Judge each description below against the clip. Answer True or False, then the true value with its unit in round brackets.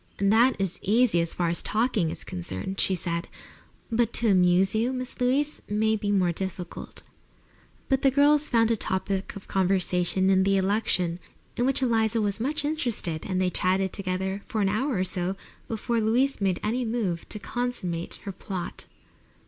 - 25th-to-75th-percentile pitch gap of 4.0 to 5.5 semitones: True (4.3 semitones)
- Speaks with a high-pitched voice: True (200 Hz)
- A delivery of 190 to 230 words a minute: False (175 wpm)